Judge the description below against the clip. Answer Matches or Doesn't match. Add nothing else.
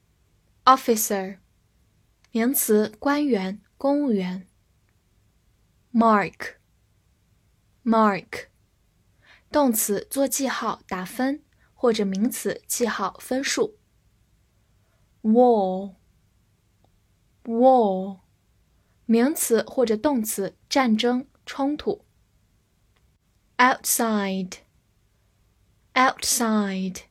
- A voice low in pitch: Doesn't match